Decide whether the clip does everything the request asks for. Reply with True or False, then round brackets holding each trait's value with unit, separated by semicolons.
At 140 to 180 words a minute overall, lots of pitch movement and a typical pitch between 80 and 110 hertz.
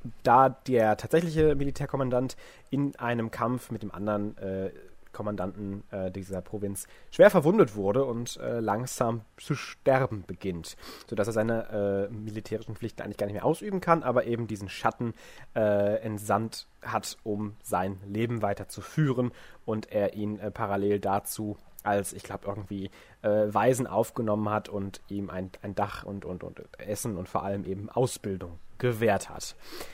False (160 wpm; 2.9 semitones; 105 Hz)